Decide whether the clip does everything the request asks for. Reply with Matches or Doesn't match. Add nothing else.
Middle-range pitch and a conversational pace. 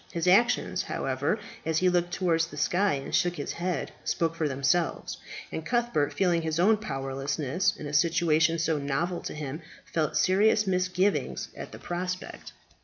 Matches